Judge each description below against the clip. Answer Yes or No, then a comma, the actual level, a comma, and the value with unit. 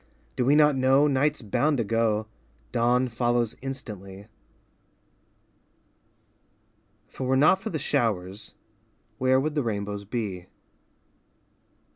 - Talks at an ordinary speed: No, slow, 115 wpm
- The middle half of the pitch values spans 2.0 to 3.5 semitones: No, average, 4.3 semitones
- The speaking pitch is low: Yes, low, 120 Hz